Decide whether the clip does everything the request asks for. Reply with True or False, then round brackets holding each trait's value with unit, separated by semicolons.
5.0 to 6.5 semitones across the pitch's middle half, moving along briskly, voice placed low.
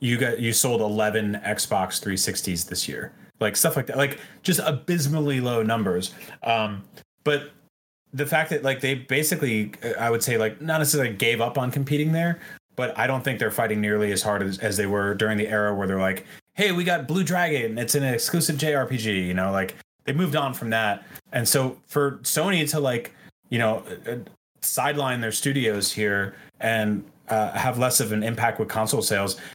False (5.4 semitones; 195 wpm; 120 Hz)